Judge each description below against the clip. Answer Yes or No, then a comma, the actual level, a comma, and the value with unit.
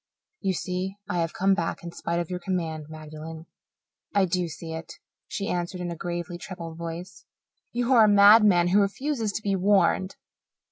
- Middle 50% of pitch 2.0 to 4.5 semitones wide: Yes, average, 2.9 semitones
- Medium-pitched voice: Yes, medium, 180 Hz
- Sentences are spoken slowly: No, average, 180 wpm